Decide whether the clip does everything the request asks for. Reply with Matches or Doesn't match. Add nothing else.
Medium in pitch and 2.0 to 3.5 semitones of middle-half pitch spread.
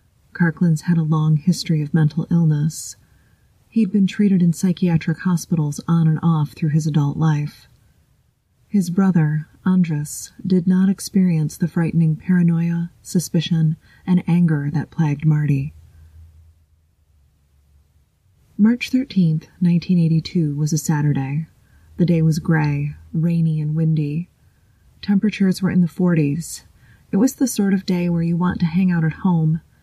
Matches